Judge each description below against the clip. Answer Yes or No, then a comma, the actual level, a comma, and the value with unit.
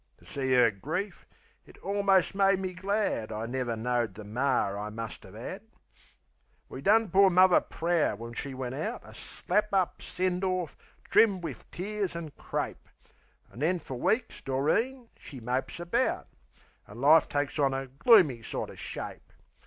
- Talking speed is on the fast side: No, average, 160 wpm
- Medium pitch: Yes, medium, 155 Hz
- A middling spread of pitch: No, wide, 7.6 semitones